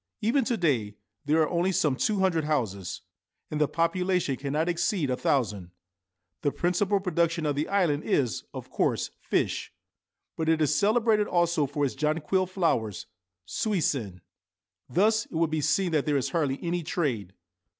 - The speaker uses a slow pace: No, average, 160 wpm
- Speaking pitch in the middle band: Yes, medium, 160 Hz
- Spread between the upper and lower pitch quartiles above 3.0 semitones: Yes, average, 4.5 semitones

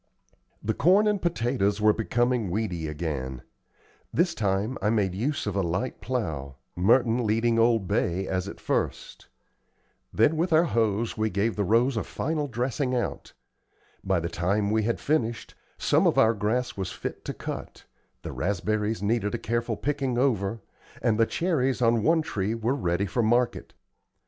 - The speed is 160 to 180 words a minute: Yes, average, 165 wpm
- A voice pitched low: Yes, low, 110 Hz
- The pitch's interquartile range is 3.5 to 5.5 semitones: Yes, average, 4.0 semitones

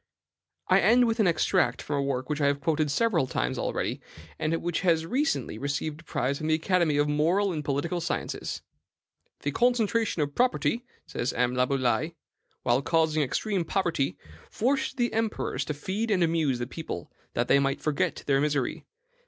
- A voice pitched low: No, medium, 155 Hz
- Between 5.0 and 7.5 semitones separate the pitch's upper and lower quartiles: Yes, wide, 5.4 semitones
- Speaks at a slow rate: No, average, 175 wpm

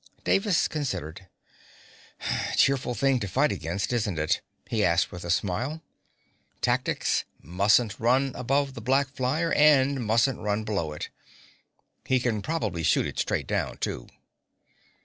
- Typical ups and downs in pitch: No, wide, 5.7 semitones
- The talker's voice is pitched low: Yes, low, 120 Hz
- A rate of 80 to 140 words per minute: Yes, slow, 135 wpm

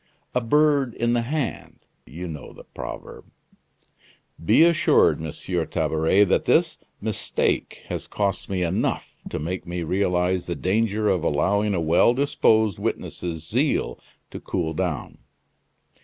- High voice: No, very low, 95 Hz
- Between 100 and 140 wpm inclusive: Yes, slow, 135 wpm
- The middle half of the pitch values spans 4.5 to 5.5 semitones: Yes, average, 5.1 semitones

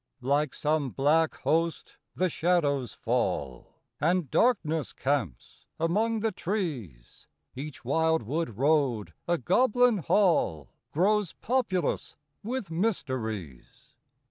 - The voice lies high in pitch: No, medium, 160 Hz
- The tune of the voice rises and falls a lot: Yes, wide, 5.9 semitones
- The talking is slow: Yes, slow, 100 wpm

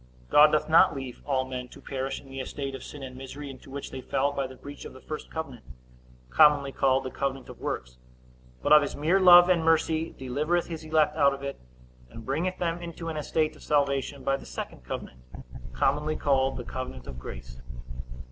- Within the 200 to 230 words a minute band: Yes, fast, 205 wpm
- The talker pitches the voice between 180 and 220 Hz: No, medium, 140 Hz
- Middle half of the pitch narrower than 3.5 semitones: Yes, average, 2.9 semitones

